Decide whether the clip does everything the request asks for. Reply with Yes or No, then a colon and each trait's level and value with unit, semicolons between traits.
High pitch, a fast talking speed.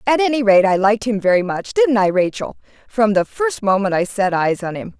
Yes: high, 210 Hz; fast, 230 wpm